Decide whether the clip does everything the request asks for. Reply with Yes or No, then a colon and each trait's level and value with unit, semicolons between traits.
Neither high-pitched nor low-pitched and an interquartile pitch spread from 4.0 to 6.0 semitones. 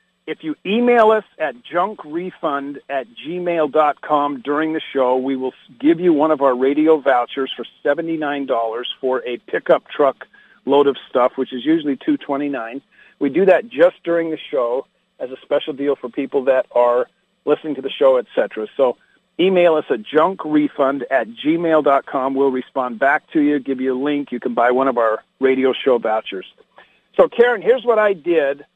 Yes: medium, 145 Hz; average, 4.7 semitones